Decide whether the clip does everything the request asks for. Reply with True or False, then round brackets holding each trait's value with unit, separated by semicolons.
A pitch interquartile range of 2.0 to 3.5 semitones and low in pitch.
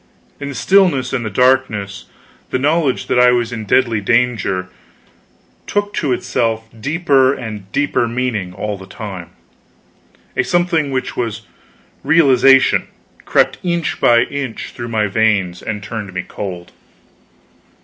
False (4.5 semitones; 120 Hz)